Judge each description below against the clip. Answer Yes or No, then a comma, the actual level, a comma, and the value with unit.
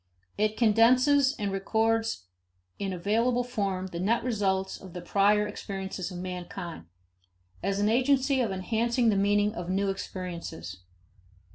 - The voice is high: Yes, high, 205 Hz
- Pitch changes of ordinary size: Yes, average, 3.4 semitones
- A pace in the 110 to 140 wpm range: Yes, slow, 135 wpm